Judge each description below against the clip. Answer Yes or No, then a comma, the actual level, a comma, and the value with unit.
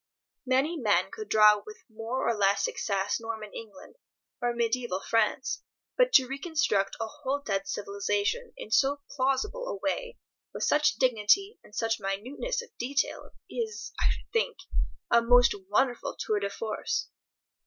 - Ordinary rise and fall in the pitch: No, wide, 5.9 semitones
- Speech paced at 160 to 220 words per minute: No, average, 150 wpm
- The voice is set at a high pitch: Yes, high, 240 Hz